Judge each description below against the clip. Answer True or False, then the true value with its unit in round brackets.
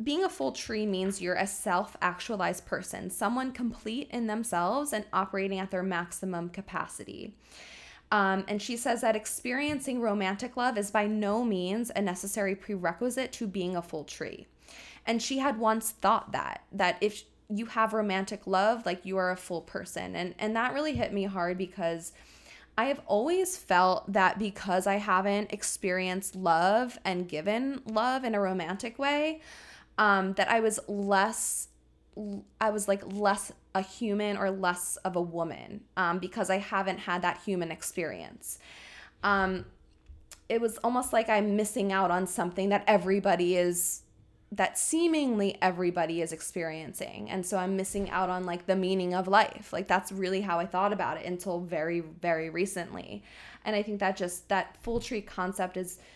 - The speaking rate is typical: True (170 wpm)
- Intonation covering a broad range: False (3.1 semitones)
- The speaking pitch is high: True (195 Hz)